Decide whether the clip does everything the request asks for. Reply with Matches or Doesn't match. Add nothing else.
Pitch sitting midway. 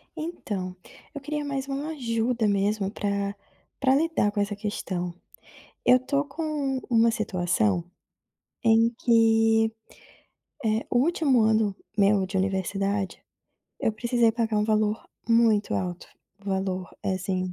Doesn't match